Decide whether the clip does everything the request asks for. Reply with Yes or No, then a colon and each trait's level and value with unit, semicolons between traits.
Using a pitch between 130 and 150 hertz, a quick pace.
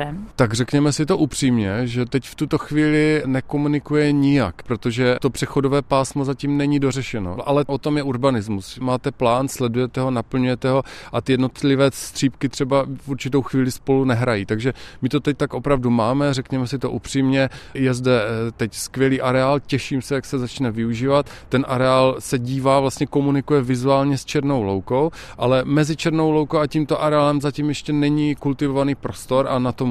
Yes: low, 135 Hz; fast, 175 wpm